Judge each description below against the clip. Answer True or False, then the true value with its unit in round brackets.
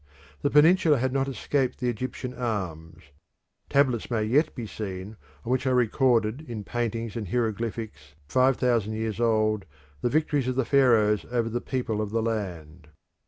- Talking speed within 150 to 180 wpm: True (165 wpm)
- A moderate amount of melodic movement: True (3.2 semitones)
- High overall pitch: False (115 Hz)